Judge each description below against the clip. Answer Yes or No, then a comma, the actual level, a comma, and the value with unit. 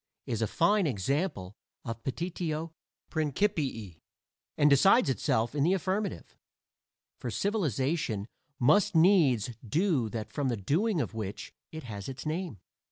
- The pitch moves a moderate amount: No, wide, 7.6 semitones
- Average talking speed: No, slow, 130 wpm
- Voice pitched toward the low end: No, medium, 150 Hz